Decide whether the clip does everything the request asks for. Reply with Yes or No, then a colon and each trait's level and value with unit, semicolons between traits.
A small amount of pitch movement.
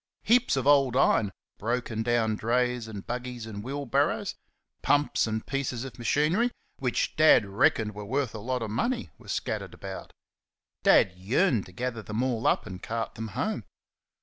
No: average, 3.6 semitones